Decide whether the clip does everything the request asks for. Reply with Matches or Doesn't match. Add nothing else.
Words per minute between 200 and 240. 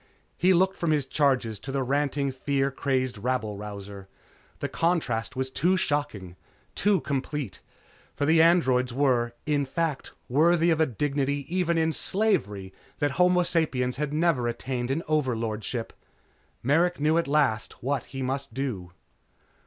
Doesn't match